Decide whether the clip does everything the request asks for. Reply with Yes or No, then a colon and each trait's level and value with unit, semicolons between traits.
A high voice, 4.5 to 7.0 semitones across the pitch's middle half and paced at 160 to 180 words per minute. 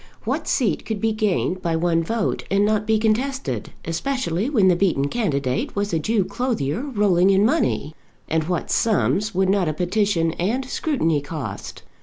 Yes: high, 195 Hz; average, 5.0 semitones; average, 170 wpm